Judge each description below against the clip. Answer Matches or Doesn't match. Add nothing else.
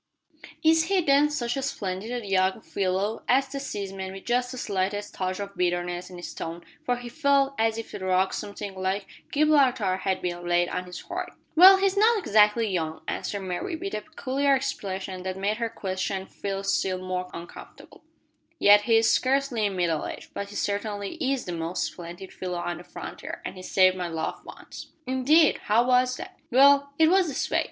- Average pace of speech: Matches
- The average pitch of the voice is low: Doesn't match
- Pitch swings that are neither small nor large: Doesn't match